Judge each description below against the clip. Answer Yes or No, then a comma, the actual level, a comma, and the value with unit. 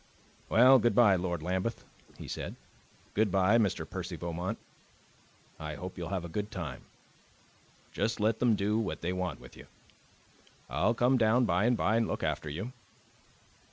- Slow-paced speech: No, average, 155 wpm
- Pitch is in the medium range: No, low, 100 Hz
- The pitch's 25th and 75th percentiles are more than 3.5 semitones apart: Yes, average, 4.5 semitones